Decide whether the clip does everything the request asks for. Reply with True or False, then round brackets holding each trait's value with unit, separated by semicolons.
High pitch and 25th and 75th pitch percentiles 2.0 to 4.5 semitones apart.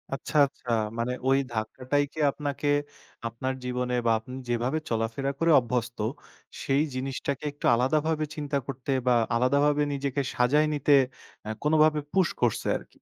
False (135 Hz; 2.9 semitones)